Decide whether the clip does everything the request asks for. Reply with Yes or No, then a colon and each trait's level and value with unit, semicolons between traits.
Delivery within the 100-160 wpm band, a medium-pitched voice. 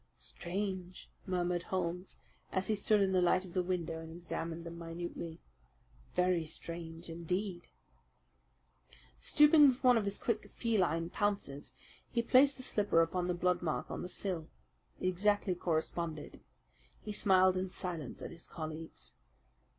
Yes: average, 145 wpm; medium, 180 Hz